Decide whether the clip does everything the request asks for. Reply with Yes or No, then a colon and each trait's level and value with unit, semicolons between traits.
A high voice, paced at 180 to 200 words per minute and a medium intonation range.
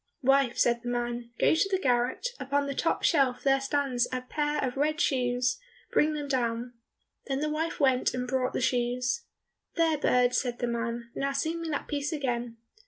Yes: very high, 260 Hz; average, 190 wpm; average, 3.2 semitones